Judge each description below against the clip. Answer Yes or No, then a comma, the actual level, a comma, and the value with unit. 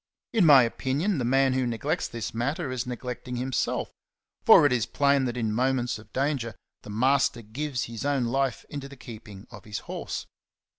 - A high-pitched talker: No, low, 125 Hz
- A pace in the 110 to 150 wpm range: No, average, 190 wpm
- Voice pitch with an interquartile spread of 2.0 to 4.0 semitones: Yes, average, 3.0 semitones